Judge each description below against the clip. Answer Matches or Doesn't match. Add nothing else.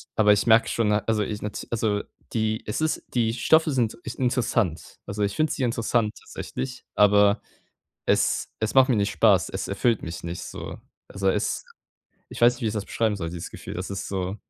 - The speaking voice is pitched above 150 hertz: Doesn't match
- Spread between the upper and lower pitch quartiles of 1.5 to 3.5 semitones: Matches